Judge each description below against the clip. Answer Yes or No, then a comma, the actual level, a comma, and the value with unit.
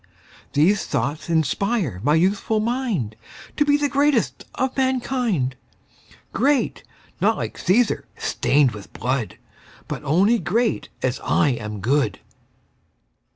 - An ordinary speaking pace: No, slow, 115 wpm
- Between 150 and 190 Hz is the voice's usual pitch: Yes, medium, 185 Hz